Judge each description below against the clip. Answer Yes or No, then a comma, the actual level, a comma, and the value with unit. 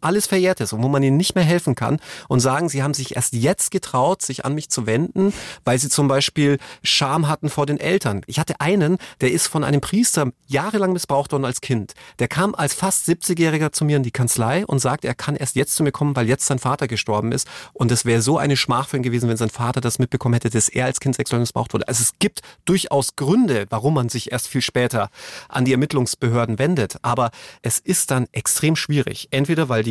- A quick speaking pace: Yes, fast, 230 wpm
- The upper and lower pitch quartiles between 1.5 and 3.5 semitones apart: No, average, 4.2 semitones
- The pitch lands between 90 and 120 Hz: No, medium, 140 Hz